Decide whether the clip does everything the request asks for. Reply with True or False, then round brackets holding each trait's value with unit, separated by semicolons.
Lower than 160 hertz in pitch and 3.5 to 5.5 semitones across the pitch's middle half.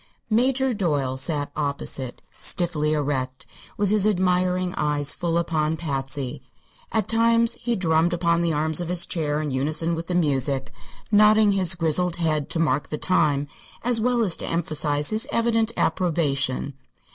False (165 Hz; 4.6 semitones)